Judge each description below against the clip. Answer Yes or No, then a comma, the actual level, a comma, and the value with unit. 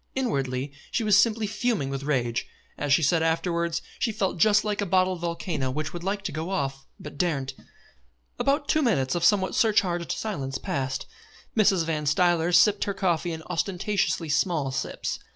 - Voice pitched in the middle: Yes, medium, 170 Hz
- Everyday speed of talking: Yes, average, 170 wpm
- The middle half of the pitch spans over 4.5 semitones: Yes, wide, 5.5 semitones